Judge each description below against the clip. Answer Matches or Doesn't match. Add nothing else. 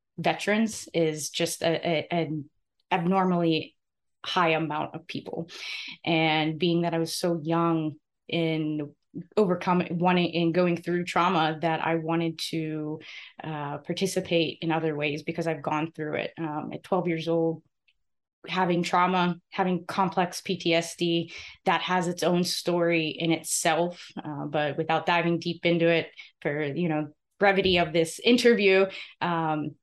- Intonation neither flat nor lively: Doesn't match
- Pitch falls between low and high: Matches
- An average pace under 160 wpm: Matches